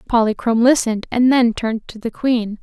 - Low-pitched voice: No, high, 230 Hz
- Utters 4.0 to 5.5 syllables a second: No, 5.8 syllables/s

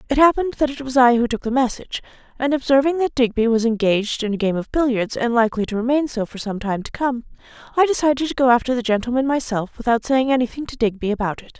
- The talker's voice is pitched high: Yes, high, 245 Hz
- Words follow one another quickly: Yes, fast, 240 wpm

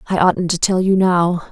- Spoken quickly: Yes, fast, 235 wpm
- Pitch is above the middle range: No, medium, 180 Hz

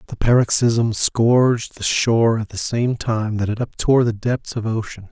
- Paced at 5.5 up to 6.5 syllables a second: No, 4.7 syllables/s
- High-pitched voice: No, low, 115 Hz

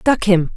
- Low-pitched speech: No, high, 200 Hz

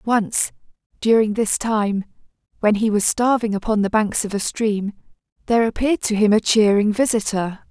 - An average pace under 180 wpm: Yes, average, 165 wpm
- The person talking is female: Yes, female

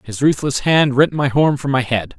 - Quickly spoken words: Yes, fast, 245 wpm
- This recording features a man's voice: Yes, male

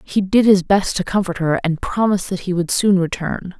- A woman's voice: Yes, female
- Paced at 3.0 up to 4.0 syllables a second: No, 5.2 syllables/s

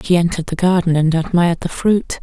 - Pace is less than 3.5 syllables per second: No, 6.1 syllables/s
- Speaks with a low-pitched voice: No, medium, 170 Hz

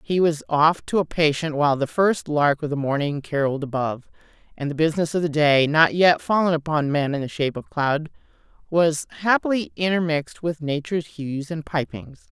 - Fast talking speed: No, average, 190 wpm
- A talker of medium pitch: Yes, medium, 155 Hz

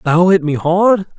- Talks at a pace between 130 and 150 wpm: No, average, 200 wpm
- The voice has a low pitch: No, medium, 175 Hz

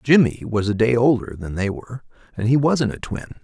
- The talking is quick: Yes, fast, 225 wpm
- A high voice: No, low, 120 Hz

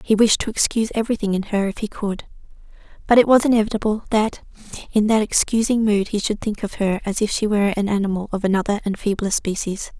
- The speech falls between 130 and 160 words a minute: No, fast, 205 wpm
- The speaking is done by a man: No, female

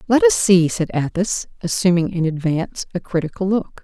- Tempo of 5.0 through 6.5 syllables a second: Yes, 5.2 syllables/s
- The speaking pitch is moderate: Yes, medium, 175 Hz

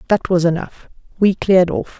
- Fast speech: No, average, 180 wpm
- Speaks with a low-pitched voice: No, medium, 185 Hz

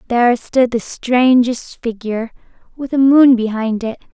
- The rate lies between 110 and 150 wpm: Yes, average, 145 wpm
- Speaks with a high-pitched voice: Yes, high, 240 Hz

